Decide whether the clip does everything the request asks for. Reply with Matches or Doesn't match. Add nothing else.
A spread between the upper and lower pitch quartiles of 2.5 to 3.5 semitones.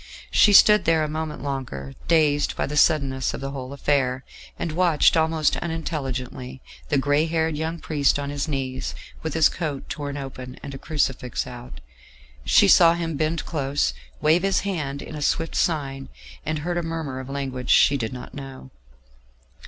Matches